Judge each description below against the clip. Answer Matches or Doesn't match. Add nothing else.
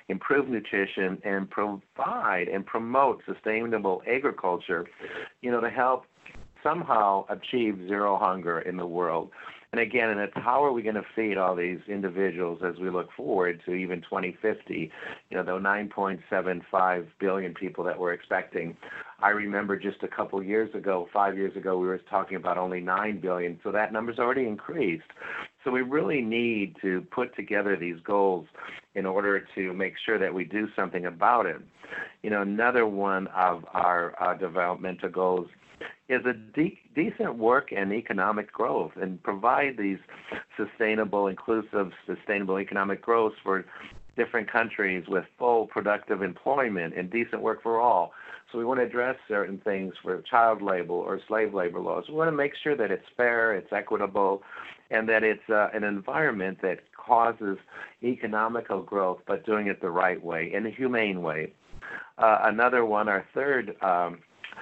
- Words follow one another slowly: Doesn't match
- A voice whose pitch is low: Matches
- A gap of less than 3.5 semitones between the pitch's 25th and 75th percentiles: Matches